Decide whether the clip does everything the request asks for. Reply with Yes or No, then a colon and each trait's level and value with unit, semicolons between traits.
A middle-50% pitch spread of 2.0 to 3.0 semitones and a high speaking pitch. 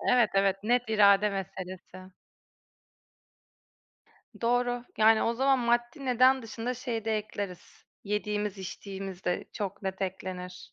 No: average, 3.7 semitones; high, 210 Hz